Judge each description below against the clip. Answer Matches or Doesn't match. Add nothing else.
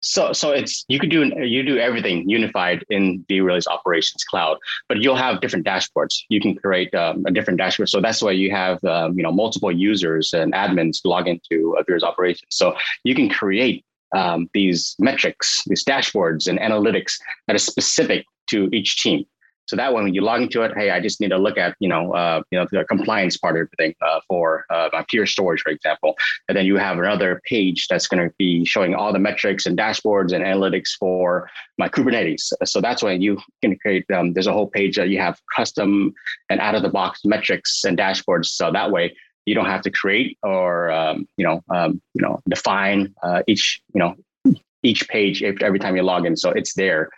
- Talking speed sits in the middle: Doesn't match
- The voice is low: Matches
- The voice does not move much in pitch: Matches